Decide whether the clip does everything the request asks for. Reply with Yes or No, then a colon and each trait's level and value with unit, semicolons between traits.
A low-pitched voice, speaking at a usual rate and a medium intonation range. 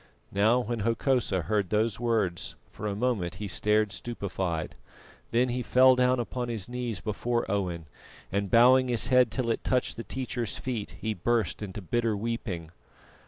Yes: low, 115 Hz; average, 160 wpm; average, 3.4 semitones